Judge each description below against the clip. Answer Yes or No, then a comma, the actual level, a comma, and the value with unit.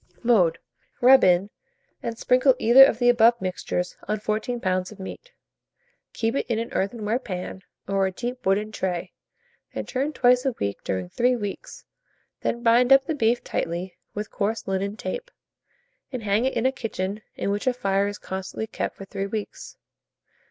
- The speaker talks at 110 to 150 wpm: No, average, 175 wpm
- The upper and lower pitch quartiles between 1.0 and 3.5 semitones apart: No, average, 4.1 semitones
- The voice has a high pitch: Yes, high, 215 Hz